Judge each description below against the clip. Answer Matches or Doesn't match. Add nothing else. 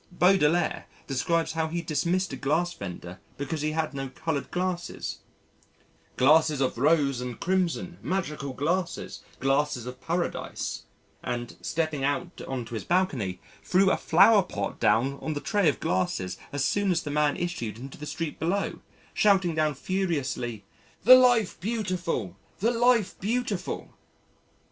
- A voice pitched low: Doesn't match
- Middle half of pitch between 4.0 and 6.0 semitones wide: Matches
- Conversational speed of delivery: Matches